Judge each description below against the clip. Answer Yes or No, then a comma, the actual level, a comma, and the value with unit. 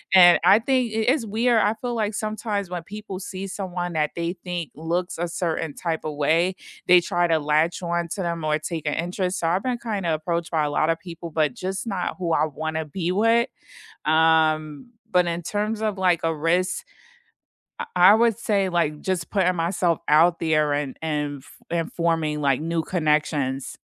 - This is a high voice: No, medium, 170 Hz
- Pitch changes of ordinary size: Yes, average, 3.3 semitones